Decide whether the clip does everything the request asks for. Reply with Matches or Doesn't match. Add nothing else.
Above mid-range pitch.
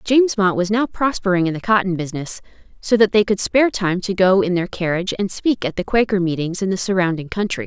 Matches